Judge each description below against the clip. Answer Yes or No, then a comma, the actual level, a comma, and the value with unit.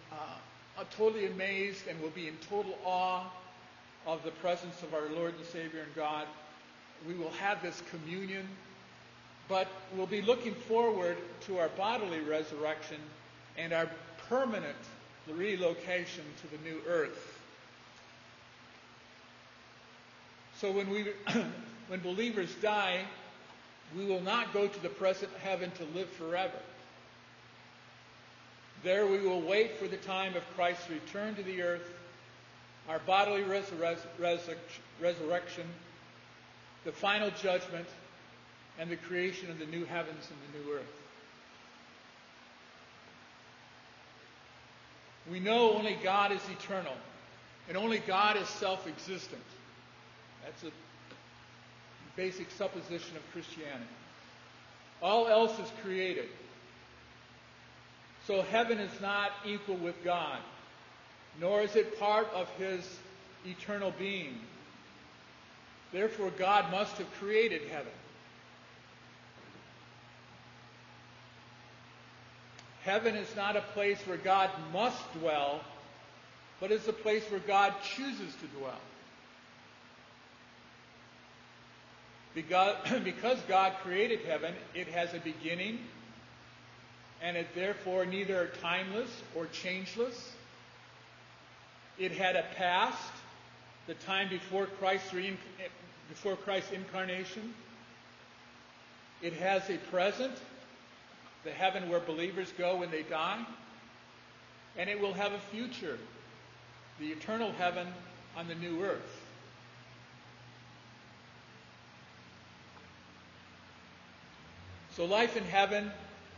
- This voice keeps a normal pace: No, slow, 110 wpm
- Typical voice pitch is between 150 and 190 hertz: Yes, medium, 185 Hz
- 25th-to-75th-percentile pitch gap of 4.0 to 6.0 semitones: No, average, 3.5 semitones